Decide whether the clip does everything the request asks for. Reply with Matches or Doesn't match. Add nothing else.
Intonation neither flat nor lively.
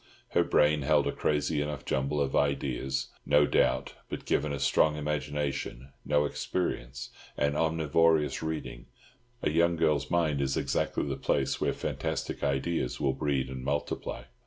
Doesn't match